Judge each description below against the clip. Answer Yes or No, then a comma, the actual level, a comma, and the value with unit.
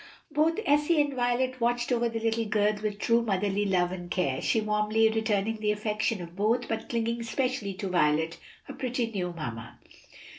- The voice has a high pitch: Yes, high, 220 Hz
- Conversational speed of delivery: Yes, average, 180 wpm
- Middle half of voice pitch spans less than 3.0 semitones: No, average, 3.5 semitones